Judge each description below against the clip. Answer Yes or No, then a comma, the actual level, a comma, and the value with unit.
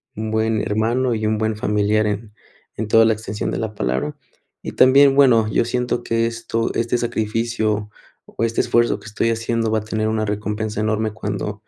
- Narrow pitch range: Yes, narrow, 1.3 semitones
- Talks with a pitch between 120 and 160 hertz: No, low, 110 Hz